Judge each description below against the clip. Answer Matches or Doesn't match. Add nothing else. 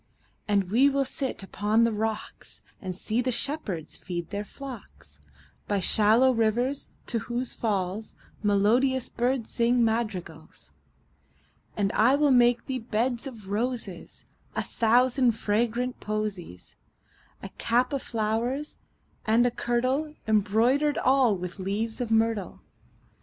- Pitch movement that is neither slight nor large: Matches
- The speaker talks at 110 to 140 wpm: Matches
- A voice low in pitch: Doesn't match